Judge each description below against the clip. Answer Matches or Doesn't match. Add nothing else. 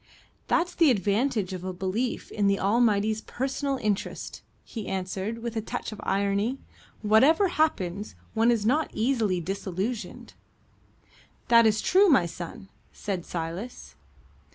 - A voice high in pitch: Matches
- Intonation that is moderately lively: Matches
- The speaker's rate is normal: Doesn't match